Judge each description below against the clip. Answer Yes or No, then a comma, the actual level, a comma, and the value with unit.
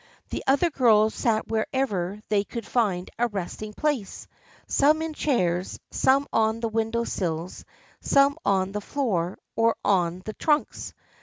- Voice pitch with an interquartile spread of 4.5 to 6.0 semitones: Yes, average, 5.3 semitones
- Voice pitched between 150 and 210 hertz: No, high, 220 Hz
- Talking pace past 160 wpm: No, average, 145 wpm